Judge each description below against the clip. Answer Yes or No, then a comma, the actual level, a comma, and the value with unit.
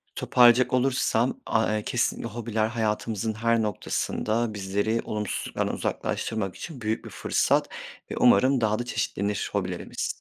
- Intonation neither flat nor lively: No, narrow, 2.0 semitones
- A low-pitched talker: Yes, low, 110 Hz